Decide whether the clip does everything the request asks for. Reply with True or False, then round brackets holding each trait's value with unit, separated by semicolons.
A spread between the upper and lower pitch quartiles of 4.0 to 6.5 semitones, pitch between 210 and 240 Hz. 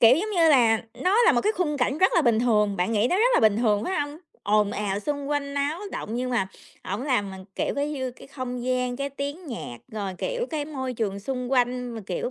False (5.0 semitones; 255 Hz)